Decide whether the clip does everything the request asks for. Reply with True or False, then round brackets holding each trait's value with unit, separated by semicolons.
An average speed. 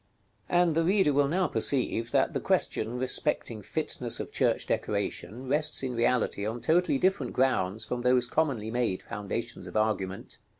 True (170 wpm)